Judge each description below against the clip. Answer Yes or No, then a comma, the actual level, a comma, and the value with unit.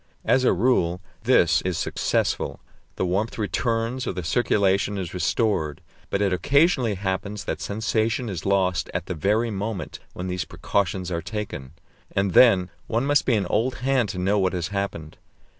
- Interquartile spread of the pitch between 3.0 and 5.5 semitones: Yes, average, 3.8 semitones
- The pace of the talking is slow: No, average, 170 wpm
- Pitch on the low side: Yes, low, 100 Hz